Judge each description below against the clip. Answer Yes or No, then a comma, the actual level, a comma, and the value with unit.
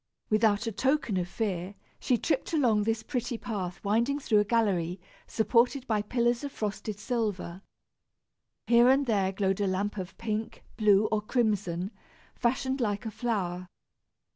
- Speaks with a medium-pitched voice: No, high, 215 Hz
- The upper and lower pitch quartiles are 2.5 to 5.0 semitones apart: Yes, average, 3.3 semitones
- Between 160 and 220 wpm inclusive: No, average, 150 wpm